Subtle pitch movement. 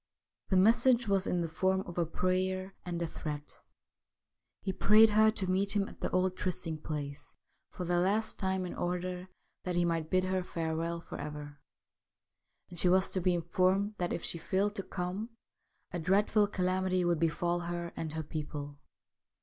Yes: narrow, 2.1 semitones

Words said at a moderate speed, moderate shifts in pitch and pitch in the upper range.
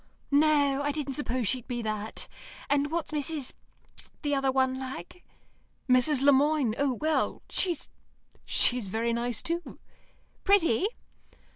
No: slow, 130 wpm; average, 3.5 semitones; very high, 275 Hz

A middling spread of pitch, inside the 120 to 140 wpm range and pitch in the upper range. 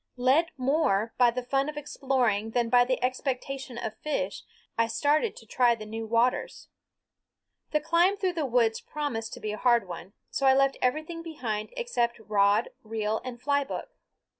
No: average, 4.3 semitones; average, 175 wpm; very high, 250 Hz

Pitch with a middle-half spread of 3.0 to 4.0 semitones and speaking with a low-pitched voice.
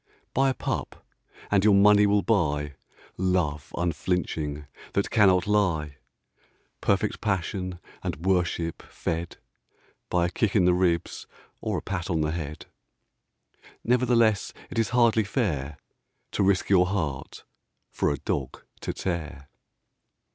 No: average, 4.6 semitones; very low, 90 Hz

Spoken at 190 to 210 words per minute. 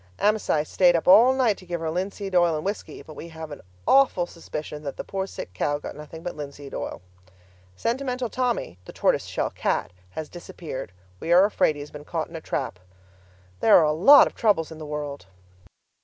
Yes: average, 200 wpm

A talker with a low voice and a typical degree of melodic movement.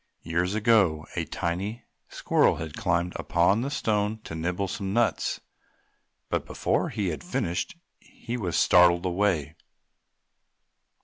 Yes: very low, 90 Hz; average, 3.7 semitones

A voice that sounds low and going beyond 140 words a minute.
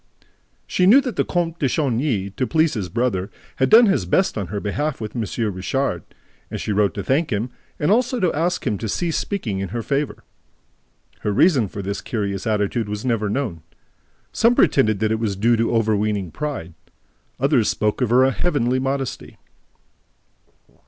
Yes: low, 115 Hz; average, 180 wpm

